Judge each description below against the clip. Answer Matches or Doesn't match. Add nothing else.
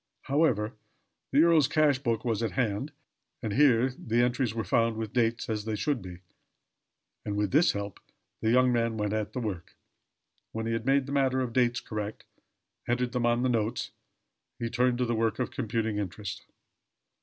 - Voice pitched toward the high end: Doesn't match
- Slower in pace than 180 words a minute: Doesn't match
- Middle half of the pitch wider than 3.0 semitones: Doesn't match